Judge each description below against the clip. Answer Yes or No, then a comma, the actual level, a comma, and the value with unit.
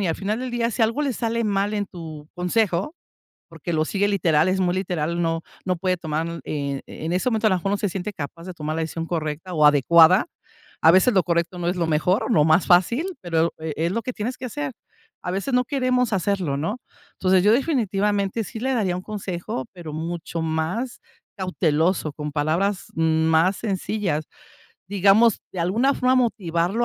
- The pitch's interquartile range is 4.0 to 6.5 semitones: Yes, average, 4.4 semitones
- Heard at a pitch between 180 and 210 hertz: Yes, medium, 185 Hz